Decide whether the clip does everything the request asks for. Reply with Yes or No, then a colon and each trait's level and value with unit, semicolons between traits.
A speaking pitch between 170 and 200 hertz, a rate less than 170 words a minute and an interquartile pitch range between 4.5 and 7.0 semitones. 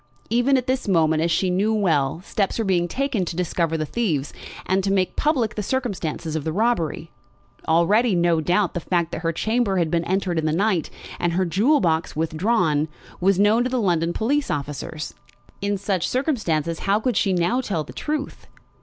No: medium, 185 Hz; average, 195 wpm; average, 5.1 semitones